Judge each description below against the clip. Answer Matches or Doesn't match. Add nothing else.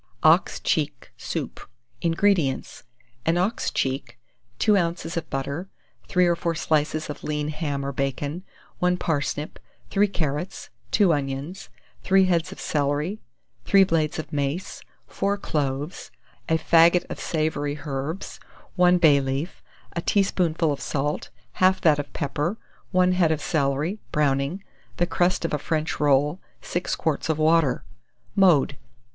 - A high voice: Doesn't match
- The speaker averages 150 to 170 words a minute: Doesn't match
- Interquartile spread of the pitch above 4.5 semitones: Doesn't match